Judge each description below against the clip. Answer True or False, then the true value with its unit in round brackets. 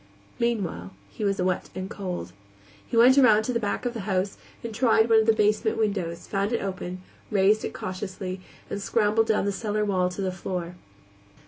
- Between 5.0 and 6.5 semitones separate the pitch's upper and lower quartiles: False (3.0 semitones)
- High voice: True (200 Hz)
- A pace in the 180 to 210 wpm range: True (195 wpm)